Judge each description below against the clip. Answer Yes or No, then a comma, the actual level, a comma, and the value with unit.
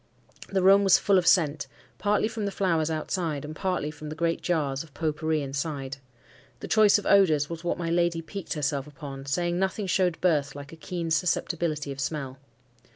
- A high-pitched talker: No, medium, 165 Hz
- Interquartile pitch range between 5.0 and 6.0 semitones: No, average, 3.6 semitones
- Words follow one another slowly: No, average, 195 wpm